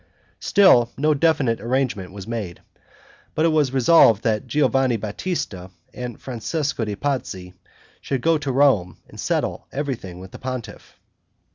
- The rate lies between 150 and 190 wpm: No, average, 140 wpm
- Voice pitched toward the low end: Yes, low, 125 Hz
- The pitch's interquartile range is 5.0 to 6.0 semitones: Yes, average, 5.3 semitones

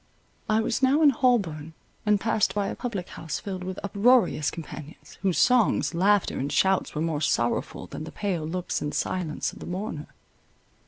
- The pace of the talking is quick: No, average, 175 wpm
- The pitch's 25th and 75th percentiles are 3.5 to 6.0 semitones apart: Yes, average, 5.0 semitones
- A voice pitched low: No, medium, 185 Hz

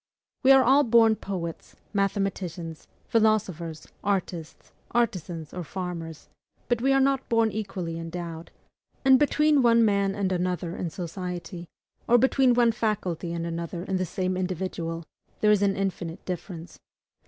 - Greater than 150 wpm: No, average, 140 wpm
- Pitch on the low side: No, high, 190 Hz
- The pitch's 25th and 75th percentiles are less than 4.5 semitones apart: No, average, 4.8 semitones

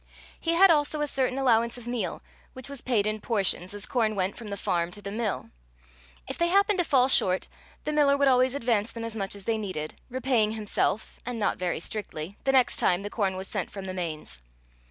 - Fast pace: Yes, fast, 220 wpm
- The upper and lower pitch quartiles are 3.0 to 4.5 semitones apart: No, average, 5.0 semitones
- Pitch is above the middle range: Yes, high, 225 Hz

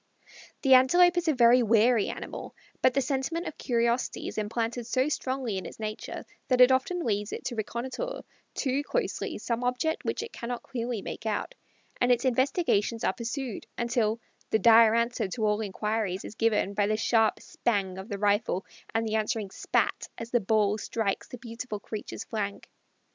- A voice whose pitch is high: Yes, high, 230 Hz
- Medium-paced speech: Yes, average, 180 wpm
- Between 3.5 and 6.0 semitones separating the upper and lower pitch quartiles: No, average, 3.1 semitones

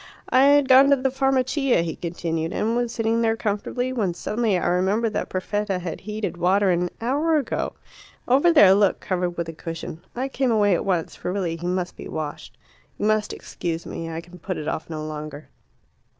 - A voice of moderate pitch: No, high, 200 Hz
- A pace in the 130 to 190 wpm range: No, average, 200 wpm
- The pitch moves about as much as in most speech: No, wide, 5.9 semitones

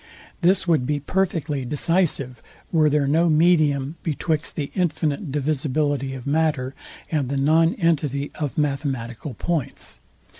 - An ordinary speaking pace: No, slow, 125 wpm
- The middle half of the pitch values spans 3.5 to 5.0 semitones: No, average, 3.0 semitones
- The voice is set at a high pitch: No, medium, 150 Hz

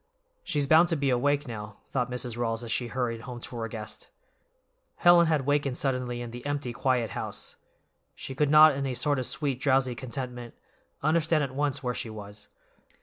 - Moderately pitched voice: No, low, 130 Hz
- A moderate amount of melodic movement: Yes, average, 3.1 semitones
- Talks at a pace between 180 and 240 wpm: Yes, average, 190 wpm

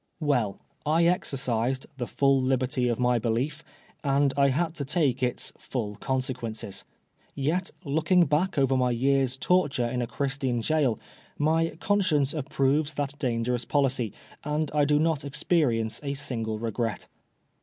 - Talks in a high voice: No, low, 135 Hz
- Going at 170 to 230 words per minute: No, average, 150 wpm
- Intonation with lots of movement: No, average, 3.3 semitones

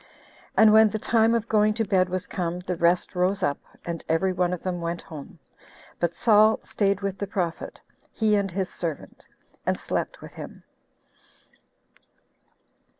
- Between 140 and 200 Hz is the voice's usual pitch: Yes, high, 190 Hz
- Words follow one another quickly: No, average, 160 wpm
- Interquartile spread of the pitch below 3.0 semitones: No, average, 3.4 semitones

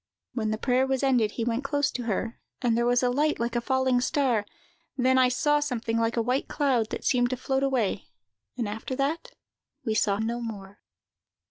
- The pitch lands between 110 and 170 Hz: No, high, 245 Hz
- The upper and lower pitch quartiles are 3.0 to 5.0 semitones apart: No, narrow, 2.6 semitones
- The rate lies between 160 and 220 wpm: Yes, fast, 205 wpm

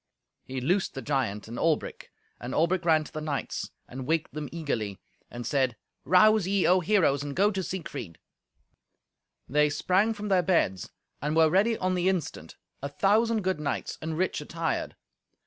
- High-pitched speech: No, medium, 160 Hz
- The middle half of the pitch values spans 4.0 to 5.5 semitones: Yes, average, 5.2 semitones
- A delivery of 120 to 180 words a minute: Yes, average, 170 wpm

